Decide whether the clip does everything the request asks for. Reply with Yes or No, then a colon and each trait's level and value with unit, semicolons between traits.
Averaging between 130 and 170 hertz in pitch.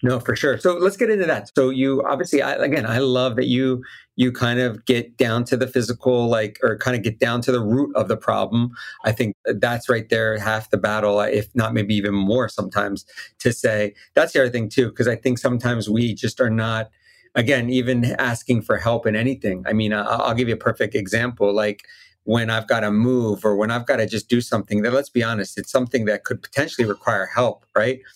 No: low, 120 Hz